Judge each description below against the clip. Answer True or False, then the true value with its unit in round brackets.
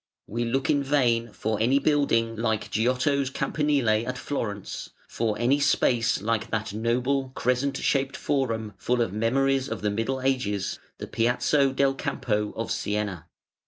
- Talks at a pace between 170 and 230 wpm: False (150 wpm)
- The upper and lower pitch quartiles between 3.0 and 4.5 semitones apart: True (3.6 semitones)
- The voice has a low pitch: True (120 Hz)